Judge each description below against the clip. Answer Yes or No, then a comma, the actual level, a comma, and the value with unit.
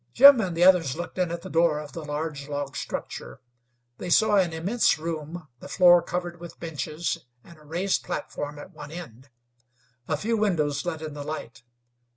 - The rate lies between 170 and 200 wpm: Yes, average, 190 wpm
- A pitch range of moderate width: Yes, average, 3.0 semitones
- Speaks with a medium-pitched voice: Yes, medium, 165 Hz